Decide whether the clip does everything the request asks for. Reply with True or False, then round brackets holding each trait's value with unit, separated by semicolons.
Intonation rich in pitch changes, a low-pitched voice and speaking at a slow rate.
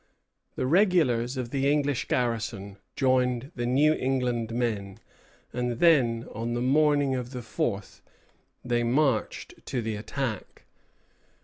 False (2.8 semitones; 125 Hz; 125 wpm)